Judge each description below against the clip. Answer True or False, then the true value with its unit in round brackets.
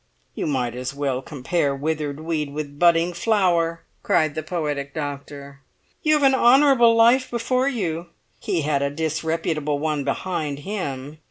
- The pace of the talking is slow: False (150 wpm)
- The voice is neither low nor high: True (155 Hz)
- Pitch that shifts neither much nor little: True (4.2 semitones)